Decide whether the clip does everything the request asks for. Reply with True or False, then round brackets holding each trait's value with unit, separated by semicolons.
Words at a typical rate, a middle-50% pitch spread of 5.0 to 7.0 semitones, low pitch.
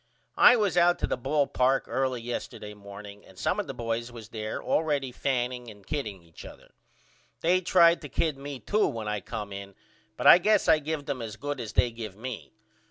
False (210 wpm; 5.6 semitones; 125 Hz)